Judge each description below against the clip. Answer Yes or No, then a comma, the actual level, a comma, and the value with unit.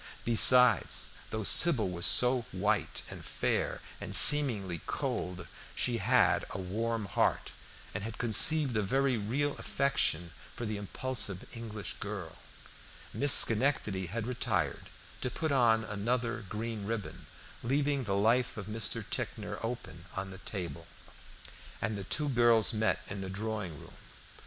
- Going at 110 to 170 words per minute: Yes, average, 140 wpm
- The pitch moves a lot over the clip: No, average, 4.0 semitones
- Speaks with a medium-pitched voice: No, low, 110 Hz